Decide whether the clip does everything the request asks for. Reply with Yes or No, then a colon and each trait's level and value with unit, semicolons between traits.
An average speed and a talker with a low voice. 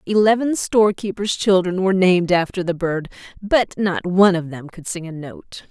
No: average, 180 wpm; medium, 185 Hz